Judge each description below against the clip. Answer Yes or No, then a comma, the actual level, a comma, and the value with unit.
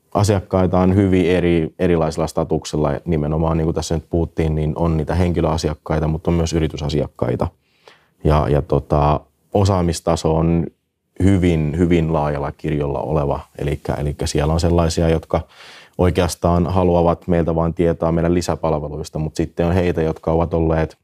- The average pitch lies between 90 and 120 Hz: No, very low, 80 Hz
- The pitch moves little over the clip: Yes, narrow, 1.8 semitones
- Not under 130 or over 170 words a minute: Yes, average, 140 wpm